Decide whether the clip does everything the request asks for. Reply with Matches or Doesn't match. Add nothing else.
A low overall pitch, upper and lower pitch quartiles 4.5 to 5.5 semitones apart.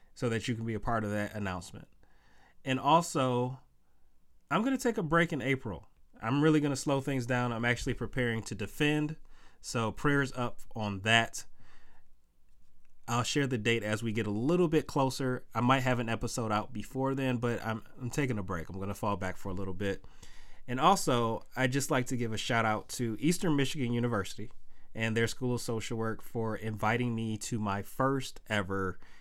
Doesn't match